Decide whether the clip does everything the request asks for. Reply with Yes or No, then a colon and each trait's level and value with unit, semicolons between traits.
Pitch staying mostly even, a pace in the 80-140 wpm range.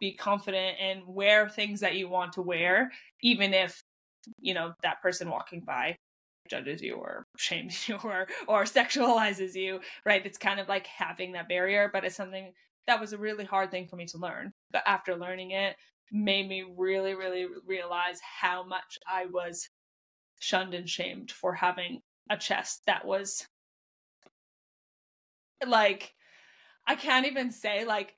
No: narrow, 2.3 semitones; average, 165 wpm